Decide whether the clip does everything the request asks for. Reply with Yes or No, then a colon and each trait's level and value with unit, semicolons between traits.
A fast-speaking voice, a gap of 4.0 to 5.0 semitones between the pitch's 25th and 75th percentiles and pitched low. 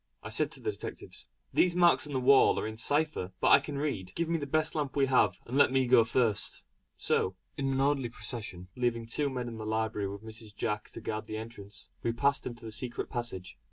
Yes: fast, 235 wpm; average, 4.4 semitones; low, 120 Hz